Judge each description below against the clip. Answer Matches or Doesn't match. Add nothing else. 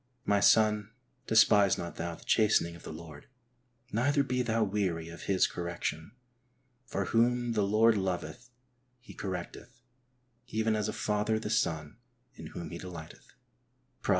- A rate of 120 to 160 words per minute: Matches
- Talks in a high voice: Doesn't match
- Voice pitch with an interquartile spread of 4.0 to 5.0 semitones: Matches